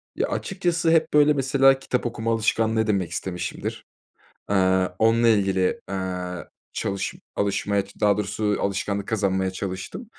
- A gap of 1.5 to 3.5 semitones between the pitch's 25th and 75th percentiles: No, average, 3.9 semitones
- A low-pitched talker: Yes, low, 105 Hz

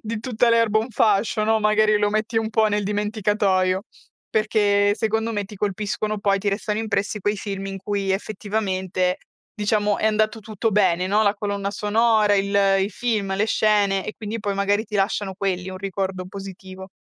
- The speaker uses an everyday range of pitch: No, narrow, 1.7 semitones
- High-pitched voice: Yes, high, 205 Hz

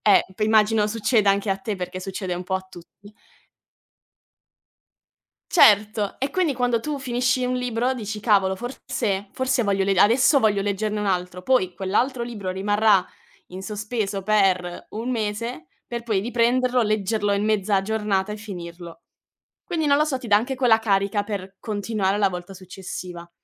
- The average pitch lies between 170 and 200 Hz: No, high, 210 Hz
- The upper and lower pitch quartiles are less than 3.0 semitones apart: No, average, 3.5 semitones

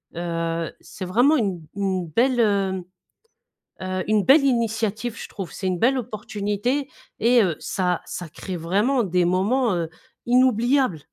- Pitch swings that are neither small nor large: Yes, average, 4.9 semitones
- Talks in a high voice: Yes, high, 205 Hz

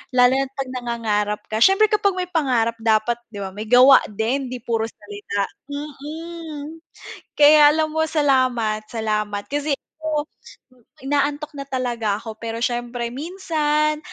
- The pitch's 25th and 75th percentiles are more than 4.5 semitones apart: Yes, average, 5.0 semitones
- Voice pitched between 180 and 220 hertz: No, very high, 255 Hz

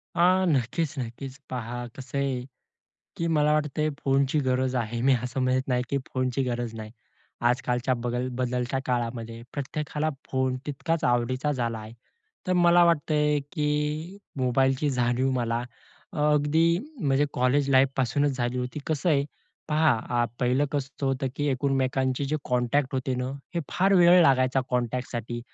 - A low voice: Yes, low, 130 Hz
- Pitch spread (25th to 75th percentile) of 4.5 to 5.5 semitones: No, average, 3.0 semitones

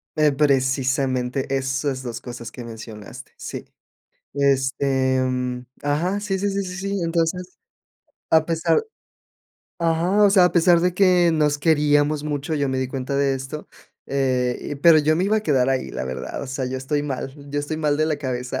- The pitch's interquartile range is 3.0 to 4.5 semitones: Yes, average, 4.0 semitones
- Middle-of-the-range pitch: Yes, medium, 145 Hz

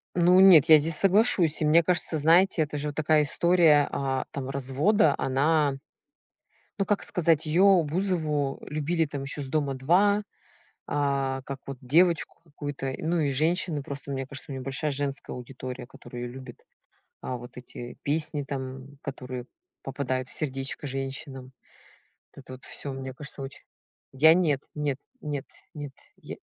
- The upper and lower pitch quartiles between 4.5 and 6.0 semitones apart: No, average, 3.2 semitones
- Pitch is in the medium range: Yes, medium, 145 Hz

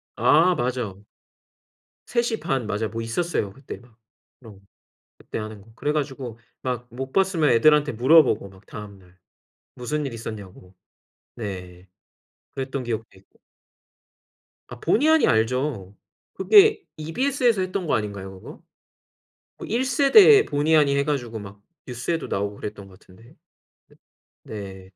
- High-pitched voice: No, low, 125 Hz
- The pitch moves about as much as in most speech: No, wide, 6.9 semitones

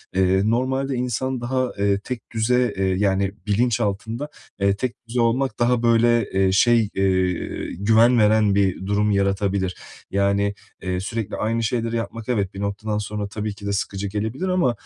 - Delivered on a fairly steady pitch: No, average, 3.1 semitones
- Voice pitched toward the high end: No, low, 105 Hz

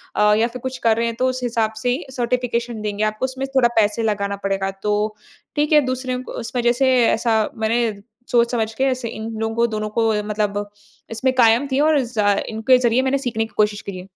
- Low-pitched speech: No, high, 230 Hz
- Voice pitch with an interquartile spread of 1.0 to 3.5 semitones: Yes, average, 2.9 semitones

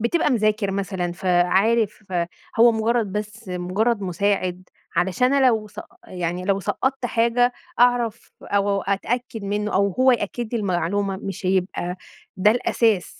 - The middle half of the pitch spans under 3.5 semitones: No, average, 3.8 semitones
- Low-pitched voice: No, high, 205 Hz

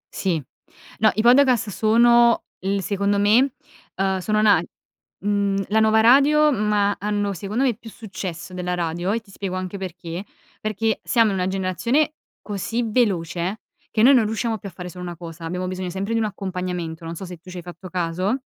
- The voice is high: Yes, high, 200 Hz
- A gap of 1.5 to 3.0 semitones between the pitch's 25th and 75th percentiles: No, average, 3.4 semitones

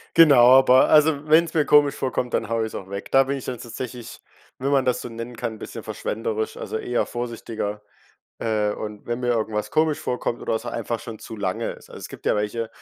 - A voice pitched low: Yes, low, 120 Hz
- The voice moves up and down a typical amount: Yes, average, 3.2 semitones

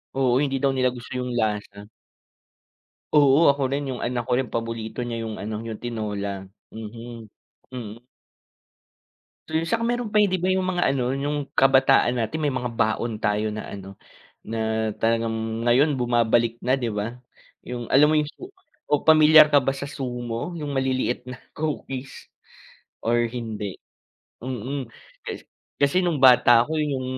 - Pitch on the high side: No, low, 125 Hz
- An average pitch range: Yes, average, 3.7 semitones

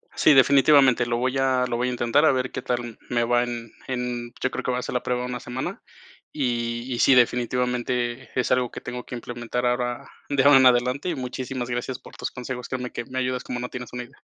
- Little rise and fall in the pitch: Yes, narrow, 1.0 semitones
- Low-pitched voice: Yes, low, 125 Hz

